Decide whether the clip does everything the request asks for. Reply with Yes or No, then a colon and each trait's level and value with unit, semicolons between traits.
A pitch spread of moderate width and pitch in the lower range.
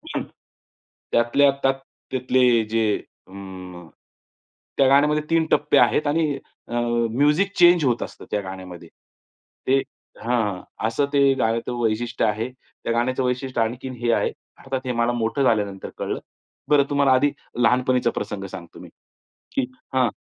Yes: average, 3.6 semitones; low, 120 Hz